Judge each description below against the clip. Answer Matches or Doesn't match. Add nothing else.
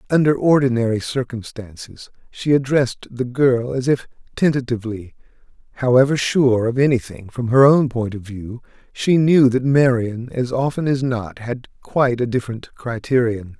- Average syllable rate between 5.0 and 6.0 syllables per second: Doesn't match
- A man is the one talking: Matches